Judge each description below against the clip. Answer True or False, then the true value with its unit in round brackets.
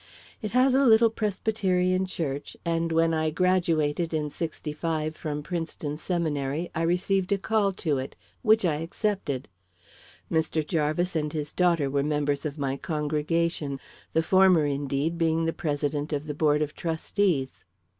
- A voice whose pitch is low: False (160 Hz)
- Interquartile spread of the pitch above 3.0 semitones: True (3.4 semitones)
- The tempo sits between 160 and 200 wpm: False (150 wpm)